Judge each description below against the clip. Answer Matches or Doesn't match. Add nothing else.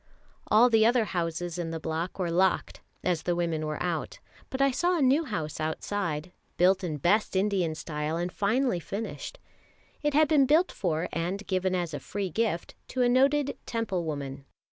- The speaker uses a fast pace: Doesn't match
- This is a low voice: Doesn't match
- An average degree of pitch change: Doesn't match